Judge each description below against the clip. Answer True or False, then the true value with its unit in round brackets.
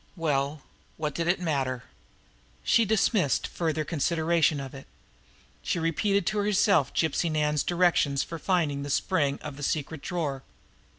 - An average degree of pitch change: True (3.7 semitones)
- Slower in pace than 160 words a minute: True (140 wpm)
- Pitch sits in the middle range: True (160 Hz)